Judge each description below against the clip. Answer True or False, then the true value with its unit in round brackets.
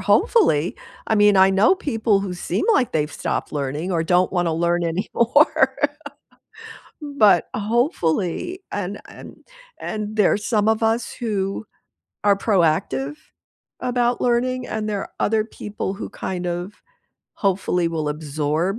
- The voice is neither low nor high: False (200 Hz)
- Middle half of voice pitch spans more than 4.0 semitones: True (4.4 semitones)